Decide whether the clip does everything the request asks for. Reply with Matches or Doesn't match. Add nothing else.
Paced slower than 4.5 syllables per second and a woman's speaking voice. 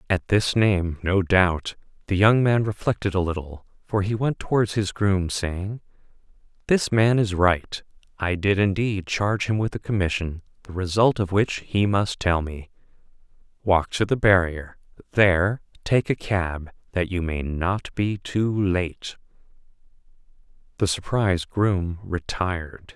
Doesn't match